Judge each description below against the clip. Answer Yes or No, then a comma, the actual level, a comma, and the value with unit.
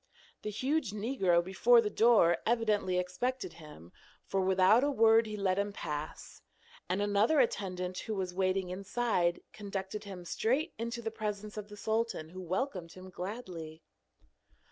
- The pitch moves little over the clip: No, average, 3.6 semitones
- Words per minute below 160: Yes, average, 150 wpm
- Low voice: No, high, 200 Hz